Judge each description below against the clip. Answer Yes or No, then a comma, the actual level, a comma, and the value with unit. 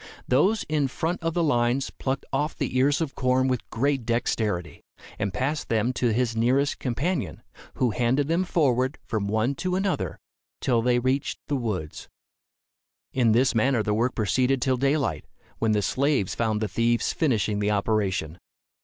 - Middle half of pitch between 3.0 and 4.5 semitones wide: Yes, average, 3.9 semitones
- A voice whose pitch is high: No, low, 125 Hz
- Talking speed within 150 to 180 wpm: Yes, average, 165 wpm